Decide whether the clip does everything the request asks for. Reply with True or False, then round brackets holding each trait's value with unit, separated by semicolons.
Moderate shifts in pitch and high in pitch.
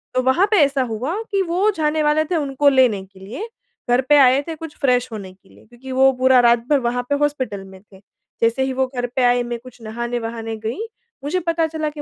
True (4.0 semitones; 260 Hz)